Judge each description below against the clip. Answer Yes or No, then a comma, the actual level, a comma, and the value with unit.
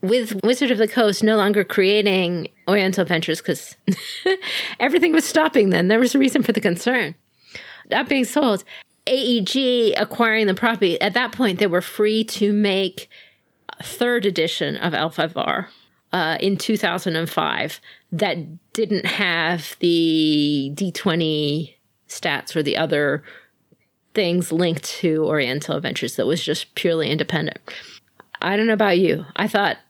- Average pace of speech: Yes, average, 145 wpm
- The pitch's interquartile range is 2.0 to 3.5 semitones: No, average, 5.1 semitones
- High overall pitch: Yes, high, 200 Hz